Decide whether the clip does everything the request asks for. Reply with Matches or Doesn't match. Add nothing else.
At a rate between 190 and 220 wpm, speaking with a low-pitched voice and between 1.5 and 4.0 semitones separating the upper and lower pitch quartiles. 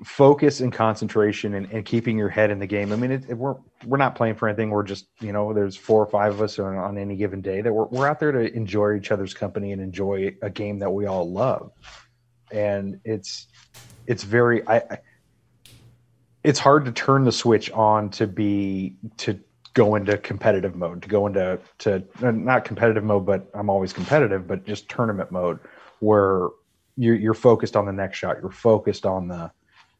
Matches